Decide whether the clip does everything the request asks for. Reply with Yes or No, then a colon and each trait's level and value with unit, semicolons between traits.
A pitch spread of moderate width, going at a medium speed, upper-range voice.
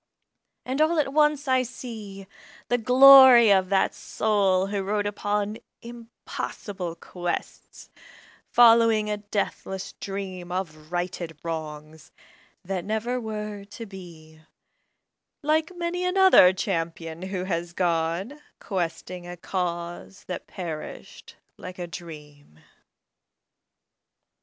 No: average, 4.8 semitones; slow, 105 wpm; high, 195 Hz